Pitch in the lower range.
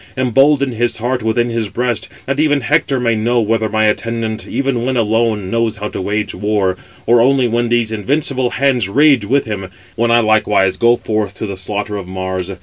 Yes: low, 115 Hz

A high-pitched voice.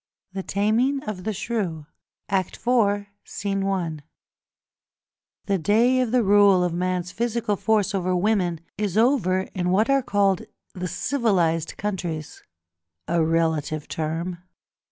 Yes: high, 195 Hz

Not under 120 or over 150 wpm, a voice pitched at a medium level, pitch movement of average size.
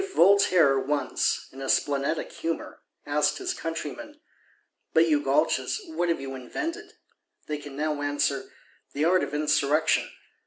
Yes: average, 140 wpm; medium, 150 Hz; average, 4.6 semitones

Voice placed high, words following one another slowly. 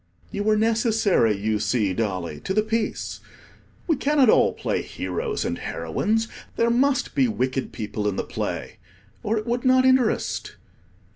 No: high, 220 Hz; average, 155 wpm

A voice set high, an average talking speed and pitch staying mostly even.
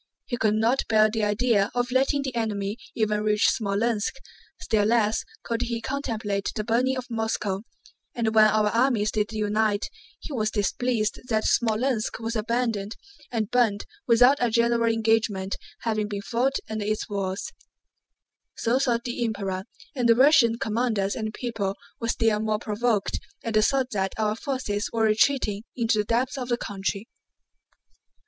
Yes: high, 225 Hz; average, 160 wpm; narrow, 2.3 semitones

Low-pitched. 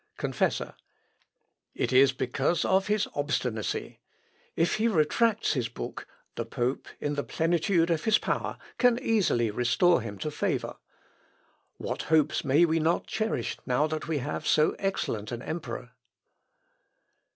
No: medium, 155 Hz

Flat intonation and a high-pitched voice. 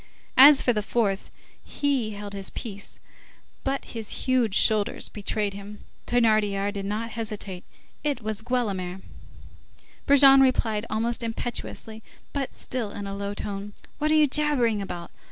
No: average, 3.5 semitones; high, 215 Hz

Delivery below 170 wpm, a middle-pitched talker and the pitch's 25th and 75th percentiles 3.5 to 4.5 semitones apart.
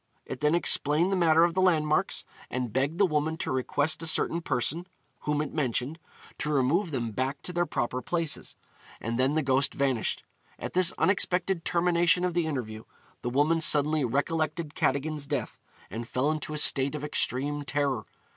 No: average, 175 wpm; medium, 150 Hz; average, 3.9 semitones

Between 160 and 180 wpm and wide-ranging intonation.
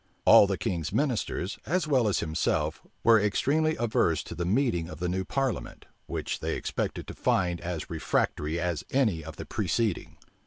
Yes: average, 170 wpm; wide, 6.3 semitones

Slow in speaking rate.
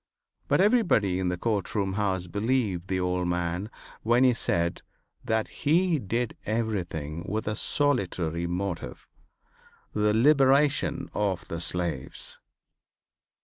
Yes: slow, 115 wpm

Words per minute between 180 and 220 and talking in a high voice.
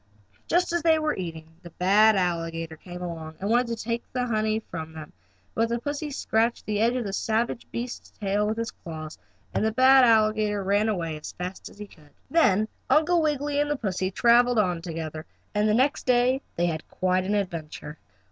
Yes: fast, 205 wpm; high, 210 Hz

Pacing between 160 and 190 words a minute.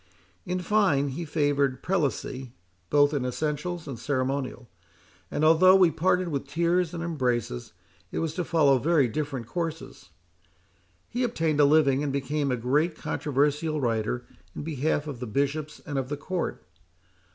No: average, 150 wpm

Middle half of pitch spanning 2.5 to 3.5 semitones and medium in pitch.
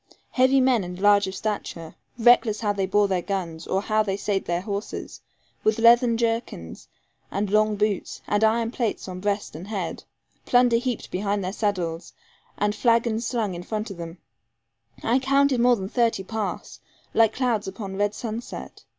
No: average, 3.2 semitones; high, 210 Hz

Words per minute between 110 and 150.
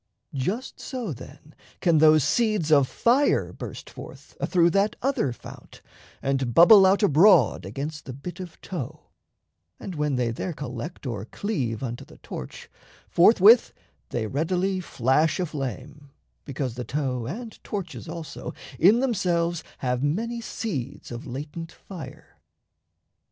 Yes: slow, 135 wpm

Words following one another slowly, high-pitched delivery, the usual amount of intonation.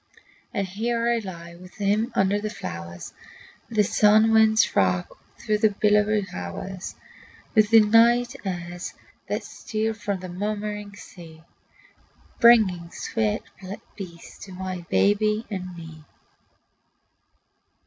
Yes: slow, 120 wpm; high, 205 Hz; average, 3.4 semitones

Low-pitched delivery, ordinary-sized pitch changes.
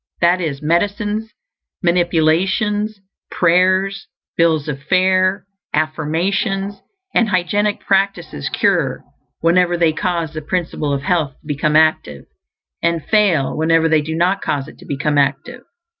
No: medium, 170 Hz; average, 3.8 semitones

